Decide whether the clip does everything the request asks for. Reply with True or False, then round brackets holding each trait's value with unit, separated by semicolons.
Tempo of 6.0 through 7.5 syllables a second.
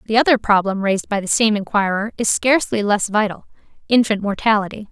True (6.1 syllables/s)